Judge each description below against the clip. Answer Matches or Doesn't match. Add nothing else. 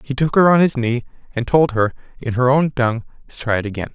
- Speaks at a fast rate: Matches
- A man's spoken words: Matches